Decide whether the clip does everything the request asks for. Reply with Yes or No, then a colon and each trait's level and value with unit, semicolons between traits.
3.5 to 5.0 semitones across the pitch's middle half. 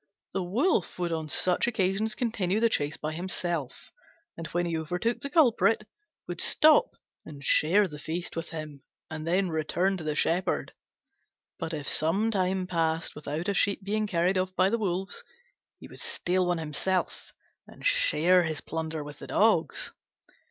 Yes: average, 3.9 semitones